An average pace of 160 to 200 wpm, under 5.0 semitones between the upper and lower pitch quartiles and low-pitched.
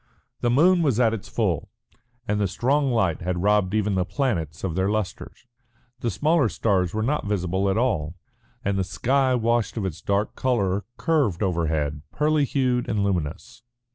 No: average, 170 wpm; average, 5.3 semitones; low, 105 Hz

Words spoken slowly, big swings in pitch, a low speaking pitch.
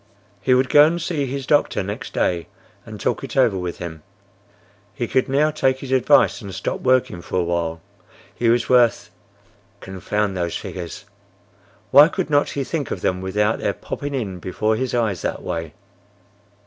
No: average, 175 wpm; wide, 6.6 semitones; low, 110 Hz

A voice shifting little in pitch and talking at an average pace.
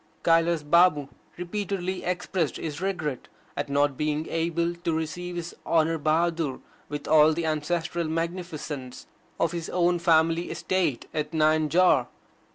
No: narrow, 2.1 semitones; slow, 130 wpm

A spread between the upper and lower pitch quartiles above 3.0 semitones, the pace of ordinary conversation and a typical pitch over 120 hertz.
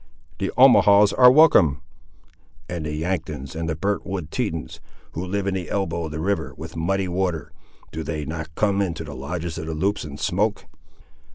No: average, 3.9 semitones; average, 185 wpm; very low, 85 Hz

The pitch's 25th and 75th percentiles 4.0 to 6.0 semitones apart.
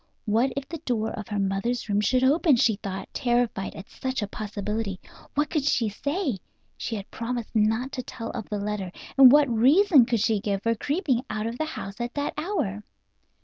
Yes: average, 4.3 semitones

